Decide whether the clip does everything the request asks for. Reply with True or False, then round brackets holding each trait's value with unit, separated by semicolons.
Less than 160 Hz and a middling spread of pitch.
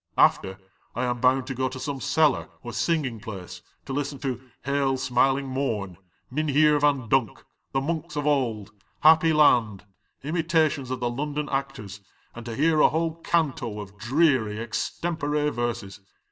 True (135 Hz; 4.0 semitones)